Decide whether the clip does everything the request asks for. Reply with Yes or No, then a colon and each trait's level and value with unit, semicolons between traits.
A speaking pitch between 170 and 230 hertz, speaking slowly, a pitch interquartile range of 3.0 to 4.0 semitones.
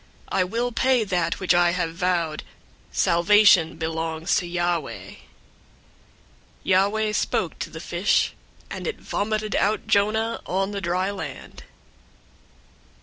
Yes: medium, 185 Hz; slow, 125 wpm; average, 3.6 semitones